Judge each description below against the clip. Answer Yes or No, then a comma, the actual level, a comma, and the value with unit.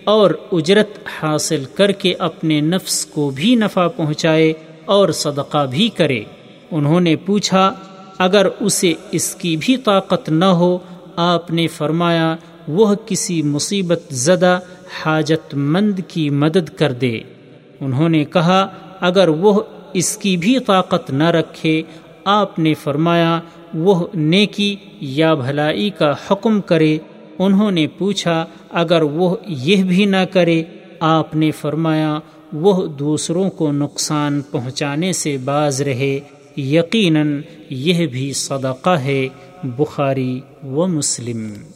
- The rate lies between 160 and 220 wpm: No, average, 125 wpm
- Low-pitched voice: No, medium, 165 Hz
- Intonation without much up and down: No, average, 3.8 semitones